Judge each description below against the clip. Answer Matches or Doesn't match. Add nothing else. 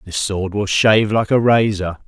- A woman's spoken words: Doesn't match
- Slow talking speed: Doesn't match